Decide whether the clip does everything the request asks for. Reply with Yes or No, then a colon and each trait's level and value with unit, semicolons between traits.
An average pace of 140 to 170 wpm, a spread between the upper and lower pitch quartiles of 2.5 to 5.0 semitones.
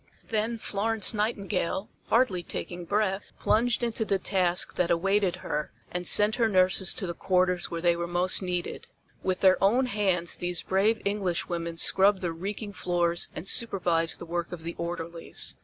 Yes: average, 165 wpm; average, 3.1 semitones